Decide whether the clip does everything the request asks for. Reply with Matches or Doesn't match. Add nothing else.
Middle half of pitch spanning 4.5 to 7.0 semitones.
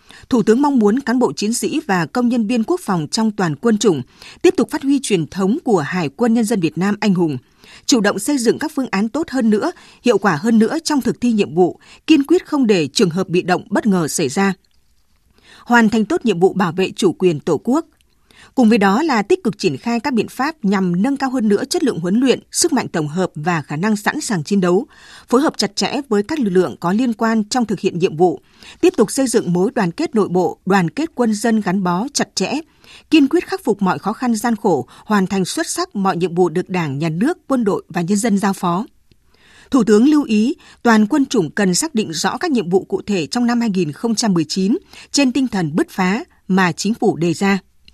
Matches